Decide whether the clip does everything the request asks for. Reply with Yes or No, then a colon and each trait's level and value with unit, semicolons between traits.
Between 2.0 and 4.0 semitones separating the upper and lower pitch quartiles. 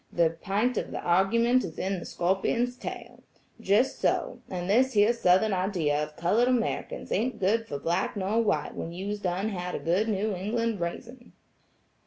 No: average, 4.4 semitones